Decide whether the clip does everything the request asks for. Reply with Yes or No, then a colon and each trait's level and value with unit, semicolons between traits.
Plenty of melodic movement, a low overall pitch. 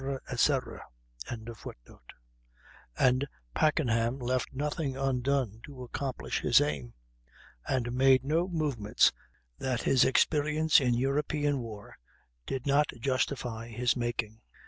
No: average, 3.4 semitones; low, 130 Hz